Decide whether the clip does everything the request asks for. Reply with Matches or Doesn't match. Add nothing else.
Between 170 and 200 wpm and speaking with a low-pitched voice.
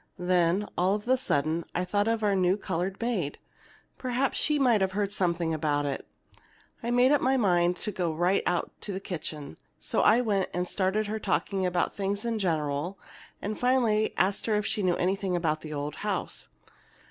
Doesn't match